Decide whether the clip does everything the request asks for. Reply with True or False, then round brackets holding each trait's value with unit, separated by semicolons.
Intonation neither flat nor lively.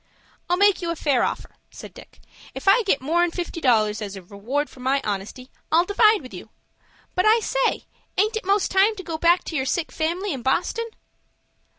False (7.2 semitones)